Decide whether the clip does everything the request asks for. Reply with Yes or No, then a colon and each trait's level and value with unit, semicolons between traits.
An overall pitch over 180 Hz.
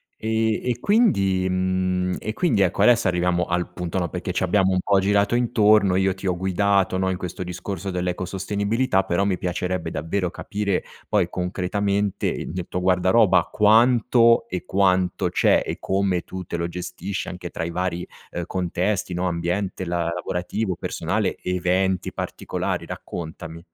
No: very low, 95 Hz